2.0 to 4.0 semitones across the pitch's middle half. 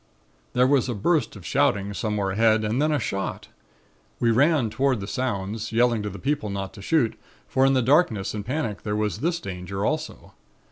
No: average, 4.9 semitones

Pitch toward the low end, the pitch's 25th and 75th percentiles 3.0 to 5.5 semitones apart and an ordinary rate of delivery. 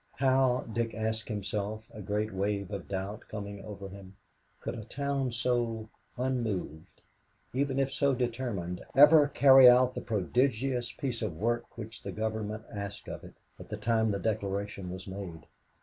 Yes: low, 110 Hz; average, 3.7 semitones; average, 160 wpm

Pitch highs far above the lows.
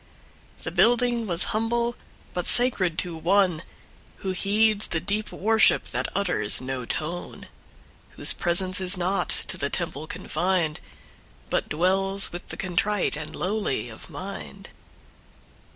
No: average, 3.6 semitones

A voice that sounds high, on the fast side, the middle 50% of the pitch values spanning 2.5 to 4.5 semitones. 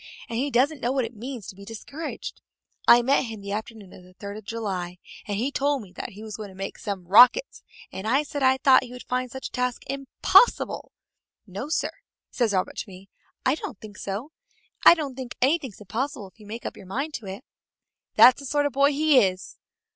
No: high, 240 Hz; fast, 225 wpm; average, 5.2 semitones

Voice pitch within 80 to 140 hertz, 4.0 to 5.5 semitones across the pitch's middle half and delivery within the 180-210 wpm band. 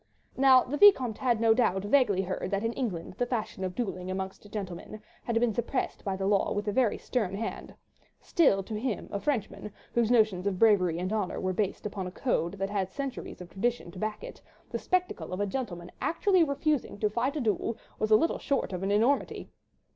No: high, 215 Hz; average, 4.4 semitones; fast, 205 wpm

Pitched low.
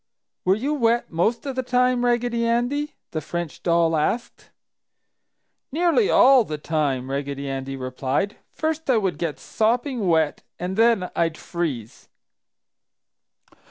No: high, 195 Hz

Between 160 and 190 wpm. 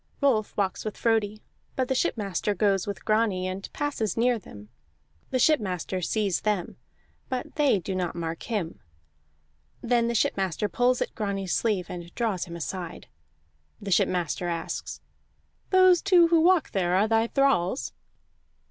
No: average, 150 wpm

